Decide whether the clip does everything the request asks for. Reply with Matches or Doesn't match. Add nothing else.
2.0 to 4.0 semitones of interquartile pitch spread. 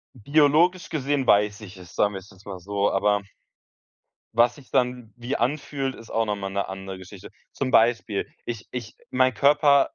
Doesn't match